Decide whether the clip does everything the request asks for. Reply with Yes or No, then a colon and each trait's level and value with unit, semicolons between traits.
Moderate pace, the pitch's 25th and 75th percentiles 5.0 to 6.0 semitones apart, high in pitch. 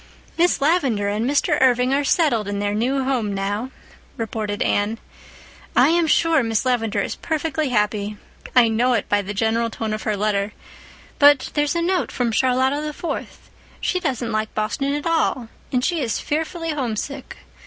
Yes: average, 165 wpm; wide, 5.4 semitones; very high, 250 Hz